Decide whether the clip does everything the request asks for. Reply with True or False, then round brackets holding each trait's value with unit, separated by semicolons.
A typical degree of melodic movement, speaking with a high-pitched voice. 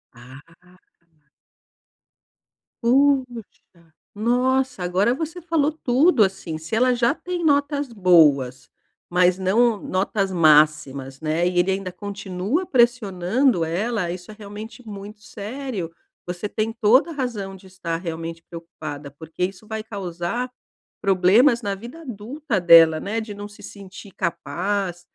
False (5.7 semitones; 200 Hz)